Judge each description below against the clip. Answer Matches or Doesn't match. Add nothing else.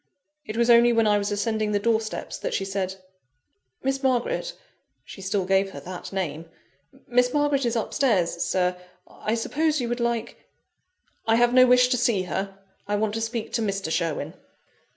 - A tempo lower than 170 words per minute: Doesn't match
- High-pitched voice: Matches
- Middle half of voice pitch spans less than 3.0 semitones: Doesn't match